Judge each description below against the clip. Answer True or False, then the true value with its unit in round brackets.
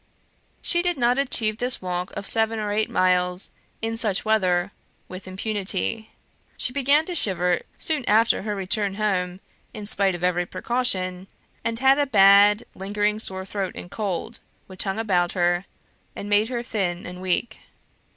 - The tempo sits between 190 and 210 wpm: False (160 wpm)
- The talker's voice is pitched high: True (205 Hz)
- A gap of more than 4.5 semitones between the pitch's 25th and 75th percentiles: False (3.5 semitones)